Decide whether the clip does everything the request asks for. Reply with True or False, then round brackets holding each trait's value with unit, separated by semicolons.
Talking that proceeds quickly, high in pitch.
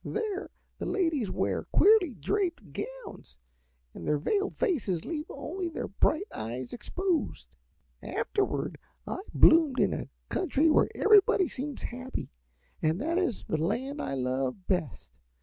False (135 wpm; 295 Hz)